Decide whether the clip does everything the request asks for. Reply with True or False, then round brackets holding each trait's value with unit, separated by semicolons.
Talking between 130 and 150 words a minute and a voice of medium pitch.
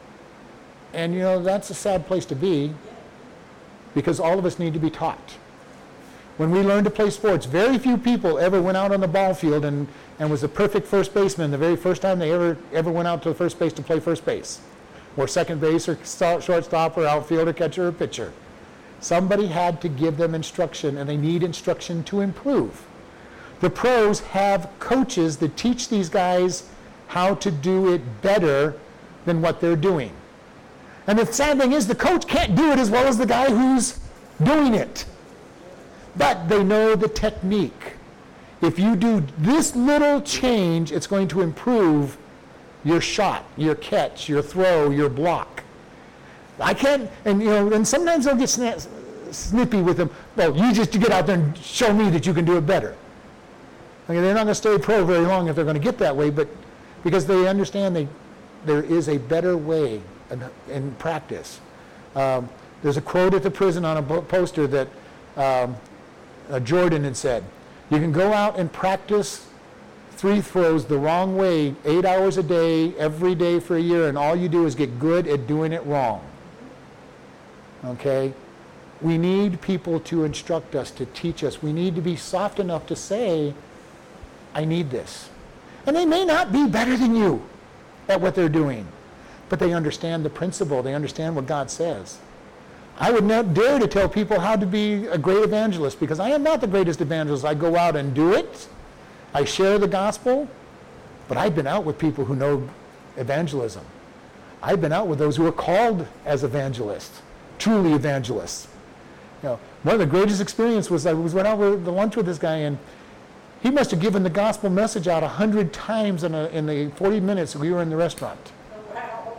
False (190 wpm; 175 Hz)